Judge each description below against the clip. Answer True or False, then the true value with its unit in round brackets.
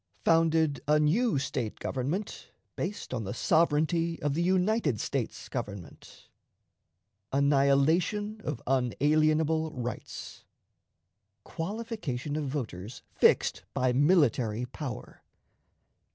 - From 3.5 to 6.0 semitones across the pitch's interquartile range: True (4.6 semitones)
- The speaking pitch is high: False (150 Hz)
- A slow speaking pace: True (95 wpm)